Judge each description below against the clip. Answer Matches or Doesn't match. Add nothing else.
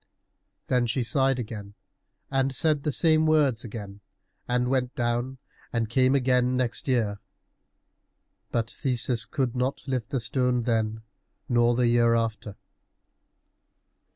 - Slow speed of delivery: Matches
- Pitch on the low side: Matches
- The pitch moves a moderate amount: Doesn't match